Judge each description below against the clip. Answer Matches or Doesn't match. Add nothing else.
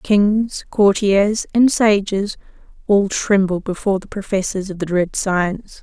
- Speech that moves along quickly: Doesn't match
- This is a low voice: Doesn't match